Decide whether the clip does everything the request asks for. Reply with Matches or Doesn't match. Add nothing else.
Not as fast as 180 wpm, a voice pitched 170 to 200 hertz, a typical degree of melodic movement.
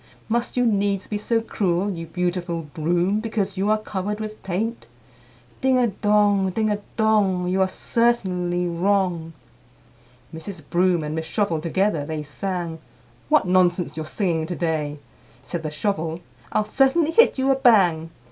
Matches